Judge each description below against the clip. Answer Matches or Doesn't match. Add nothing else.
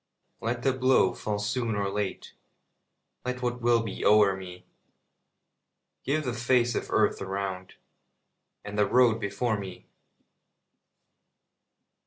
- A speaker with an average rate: Doesn't match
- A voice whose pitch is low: Matches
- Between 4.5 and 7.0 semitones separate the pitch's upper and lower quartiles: Doesn't match